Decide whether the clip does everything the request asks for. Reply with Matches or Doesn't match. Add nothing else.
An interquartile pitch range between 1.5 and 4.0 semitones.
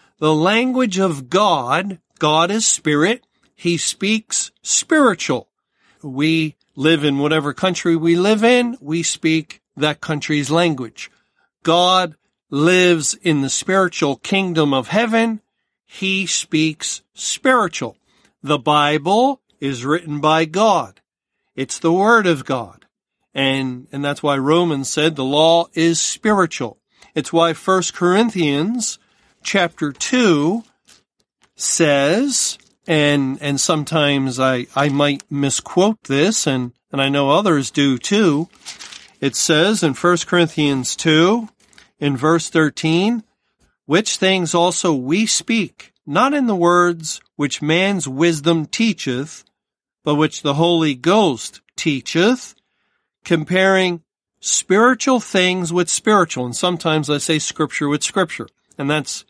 Doesn't match